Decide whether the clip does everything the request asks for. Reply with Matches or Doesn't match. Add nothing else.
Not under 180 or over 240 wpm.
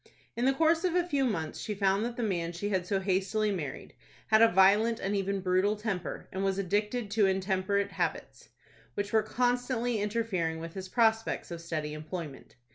Matches